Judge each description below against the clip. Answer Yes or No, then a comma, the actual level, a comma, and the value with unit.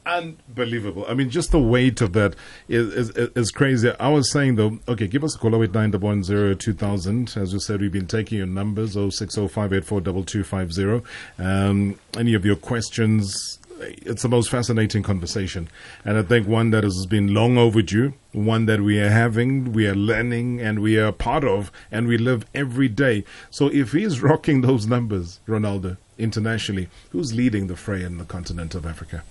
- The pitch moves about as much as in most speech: Yes, average, 3.1 semitones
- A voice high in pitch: No, low, 110 Hz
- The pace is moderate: Yes, average, 175 wpm